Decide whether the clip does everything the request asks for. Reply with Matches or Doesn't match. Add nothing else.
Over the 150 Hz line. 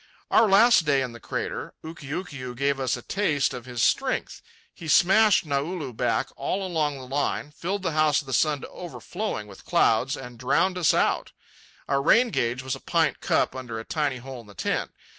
Doesn't match